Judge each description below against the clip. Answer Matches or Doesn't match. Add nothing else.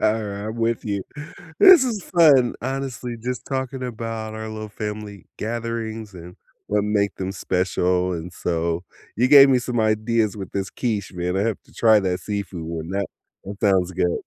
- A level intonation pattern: Doesn't match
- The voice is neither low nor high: Doesn't match